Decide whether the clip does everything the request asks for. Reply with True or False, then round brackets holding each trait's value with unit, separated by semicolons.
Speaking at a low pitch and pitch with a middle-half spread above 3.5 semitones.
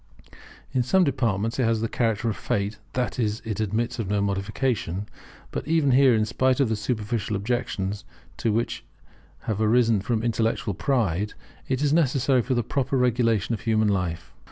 False (115 Hz; 3.2 semitones)